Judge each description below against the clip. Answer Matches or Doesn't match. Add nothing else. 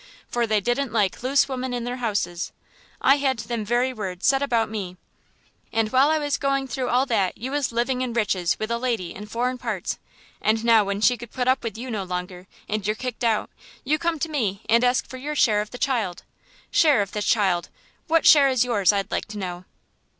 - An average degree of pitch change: Matches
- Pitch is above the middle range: Matches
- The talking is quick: Matches